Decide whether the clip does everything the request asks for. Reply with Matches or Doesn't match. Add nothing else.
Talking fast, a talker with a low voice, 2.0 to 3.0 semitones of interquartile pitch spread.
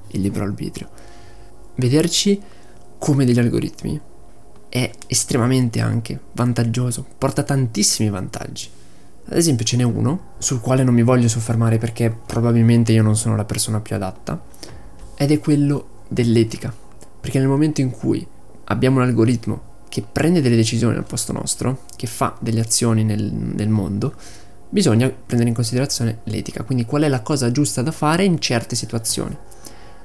Doesn't match